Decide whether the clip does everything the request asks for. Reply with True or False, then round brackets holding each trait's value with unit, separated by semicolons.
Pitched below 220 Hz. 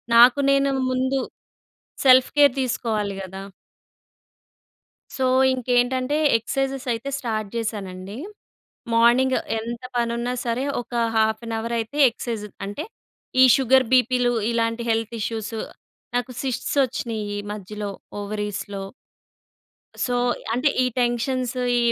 False (235 Hz)